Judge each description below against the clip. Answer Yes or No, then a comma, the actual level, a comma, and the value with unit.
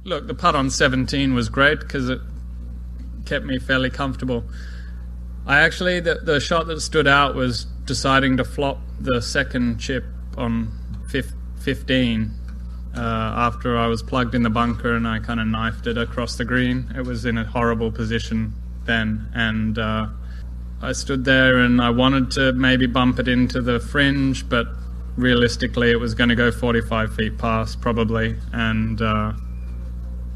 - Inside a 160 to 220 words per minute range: Yes, average, 165 wpm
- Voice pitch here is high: No, low, 115 Hz